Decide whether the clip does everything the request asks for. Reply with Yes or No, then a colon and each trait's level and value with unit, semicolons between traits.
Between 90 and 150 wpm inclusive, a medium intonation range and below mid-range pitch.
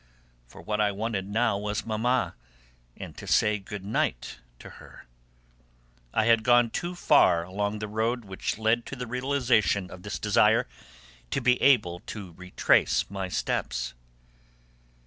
Yes: average, 145 wpm; average, 3.4 semitones; low, 105 Hz